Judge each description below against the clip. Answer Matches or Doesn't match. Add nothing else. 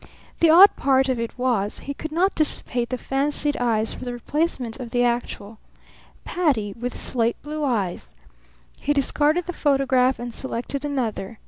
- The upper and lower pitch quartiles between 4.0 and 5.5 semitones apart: Doesn't match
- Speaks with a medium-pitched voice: Doesn't match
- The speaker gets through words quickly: Doesn't match